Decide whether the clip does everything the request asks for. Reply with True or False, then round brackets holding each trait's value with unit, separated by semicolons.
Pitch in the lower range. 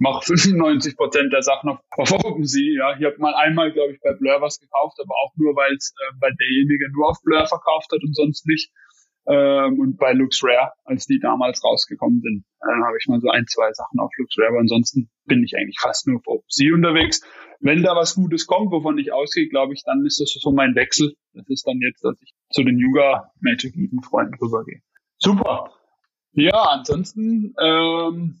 False (155 Hz)